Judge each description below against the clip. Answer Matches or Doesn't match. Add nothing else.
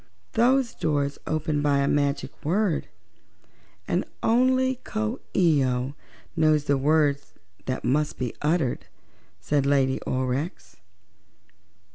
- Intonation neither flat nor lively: Matches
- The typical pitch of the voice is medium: Matches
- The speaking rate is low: Matches